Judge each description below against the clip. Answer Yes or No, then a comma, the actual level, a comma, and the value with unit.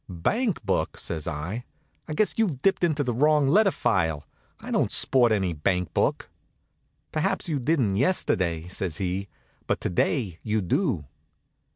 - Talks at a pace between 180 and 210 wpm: No, average, 155 wpm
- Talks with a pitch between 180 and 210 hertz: No, low, 110 Hz